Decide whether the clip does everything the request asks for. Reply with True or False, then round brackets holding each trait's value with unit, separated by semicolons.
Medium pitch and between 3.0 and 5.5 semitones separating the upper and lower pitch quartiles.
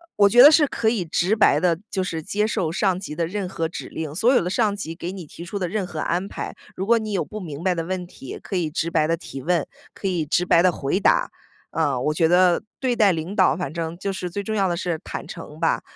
True (180 Hz; 3.5 semitones)